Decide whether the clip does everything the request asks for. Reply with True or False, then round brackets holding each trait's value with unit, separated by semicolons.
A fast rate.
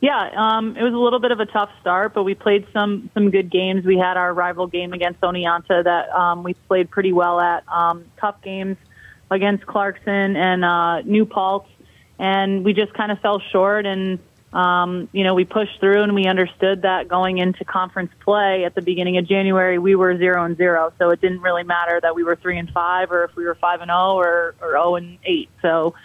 True (220 wpm)